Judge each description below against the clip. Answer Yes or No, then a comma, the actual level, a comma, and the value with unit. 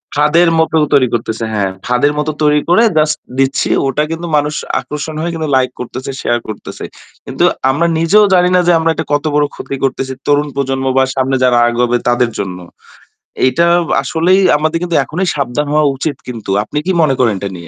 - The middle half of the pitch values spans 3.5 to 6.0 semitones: Yes, average, 4.2 semitones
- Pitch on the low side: No, medium, 145 Hz